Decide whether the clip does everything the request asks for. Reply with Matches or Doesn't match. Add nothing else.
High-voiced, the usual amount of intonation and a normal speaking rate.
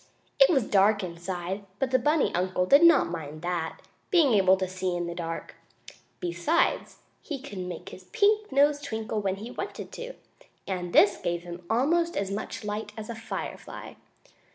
Doesn't match